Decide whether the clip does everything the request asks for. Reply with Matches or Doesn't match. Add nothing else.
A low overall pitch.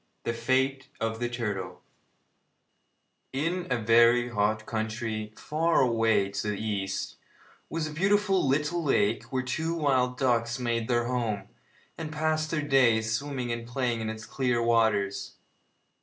Matches